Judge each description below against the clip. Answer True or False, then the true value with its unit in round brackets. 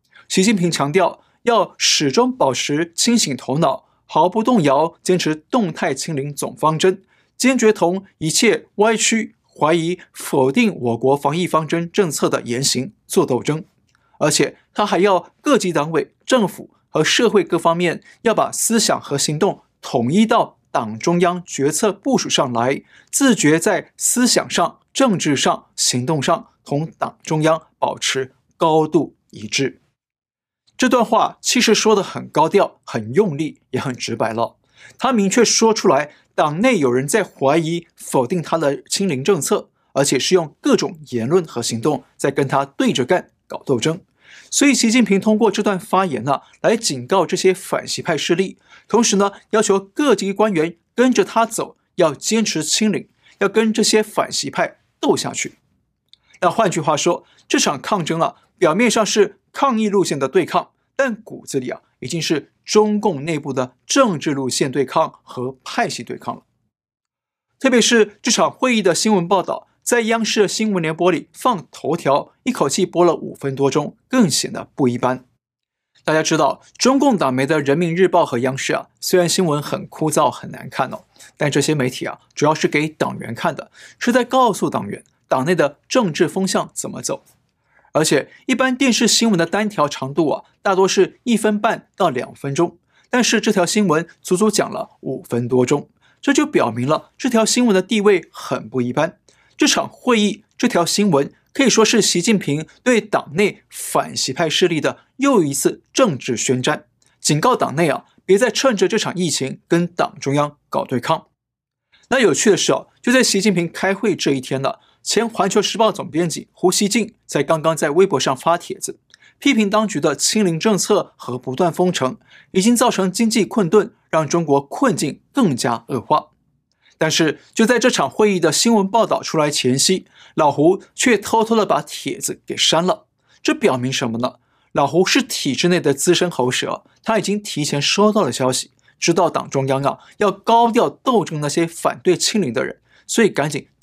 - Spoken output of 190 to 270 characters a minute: True (255 characters per minute)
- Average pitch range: False (6.4 semitones)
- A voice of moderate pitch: True (180 Hz)